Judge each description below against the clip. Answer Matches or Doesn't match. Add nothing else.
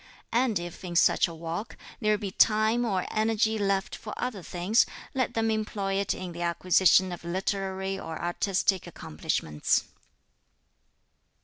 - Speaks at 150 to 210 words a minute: Doesn't match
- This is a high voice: Matches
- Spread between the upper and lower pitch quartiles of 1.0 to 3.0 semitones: Doesn't match